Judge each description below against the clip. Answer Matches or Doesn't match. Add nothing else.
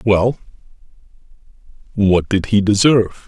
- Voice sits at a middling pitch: Doesn't match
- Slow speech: Matches